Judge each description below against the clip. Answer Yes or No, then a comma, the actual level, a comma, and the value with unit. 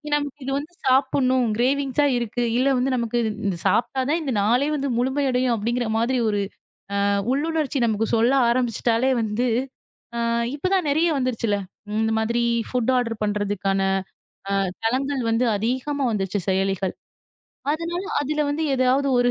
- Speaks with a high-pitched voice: Yes, very high, 250 Hz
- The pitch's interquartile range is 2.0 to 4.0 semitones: Yes, average, 3.7 semitones